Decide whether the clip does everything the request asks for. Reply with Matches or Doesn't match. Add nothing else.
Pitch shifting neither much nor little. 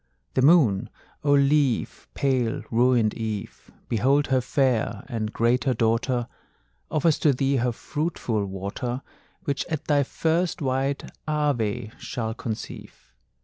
Matches